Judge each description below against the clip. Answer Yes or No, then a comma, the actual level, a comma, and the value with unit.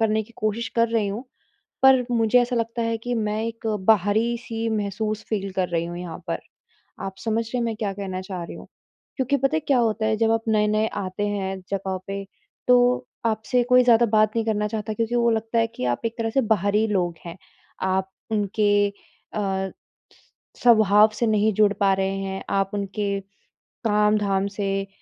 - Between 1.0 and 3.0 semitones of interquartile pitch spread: Yes, narrow, 2.5 semitones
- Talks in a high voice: Yes, high, 215 Hz